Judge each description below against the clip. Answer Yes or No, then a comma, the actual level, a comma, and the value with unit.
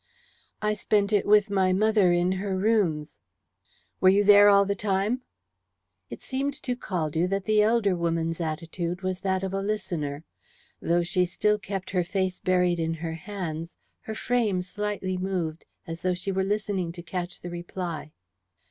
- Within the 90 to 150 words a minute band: No, average, 165 wpm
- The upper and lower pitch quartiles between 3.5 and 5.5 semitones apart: No, average, 3.0 semitones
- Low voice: No, medium, 185 Hz